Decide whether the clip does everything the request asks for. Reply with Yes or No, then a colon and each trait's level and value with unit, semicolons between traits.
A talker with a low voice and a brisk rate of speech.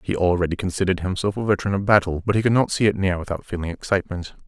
Yes: very low, 95 Hz; fast, 240 wpm